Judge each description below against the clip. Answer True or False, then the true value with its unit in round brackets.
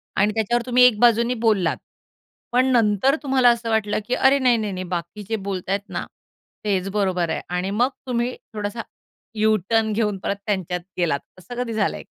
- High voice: True (215 Hz)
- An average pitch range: True (3.5 semitones)